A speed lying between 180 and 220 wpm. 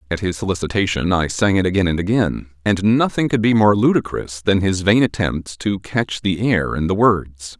Yes: fast, 205 wpm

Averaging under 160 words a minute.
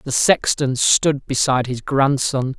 Yes: average, 140 wpm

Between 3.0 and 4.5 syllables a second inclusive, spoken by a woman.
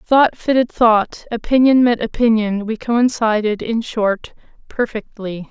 Yes: 4.0 syllables/s; female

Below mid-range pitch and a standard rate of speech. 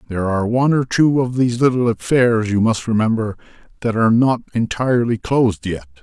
Yes: low, 115 Hz; average, 180 wpm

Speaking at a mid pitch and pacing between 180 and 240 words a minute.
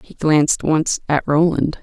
No: medium, 155 Hz; average, 165 wpm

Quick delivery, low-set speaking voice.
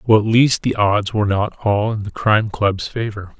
Yes: fast, 230 wpm; low, 105 Hz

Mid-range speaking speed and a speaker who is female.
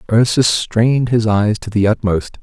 No: average, 175 wpm; male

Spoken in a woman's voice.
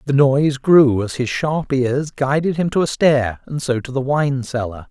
No: male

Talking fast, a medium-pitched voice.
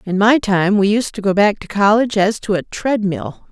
No: fast, 240 wpm; high, 205 Hz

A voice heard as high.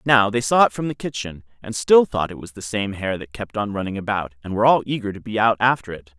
No: low, 110 Hz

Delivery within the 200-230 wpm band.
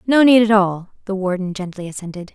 Yes: fast, 205 wpm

